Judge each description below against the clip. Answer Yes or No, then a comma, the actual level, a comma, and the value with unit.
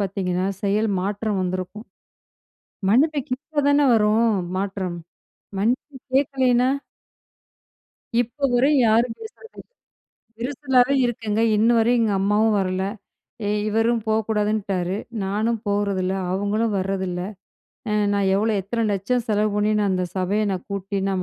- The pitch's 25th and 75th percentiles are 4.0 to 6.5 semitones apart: No, average, 3.4 semitones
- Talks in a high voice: Yes, high, 210 Hz